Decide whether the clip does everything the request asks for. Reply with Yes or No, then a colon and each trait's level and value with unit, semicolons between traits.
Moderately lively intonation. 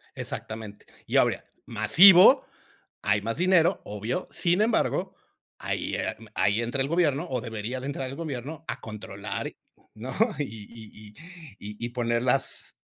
No: wide, 6.2 semitones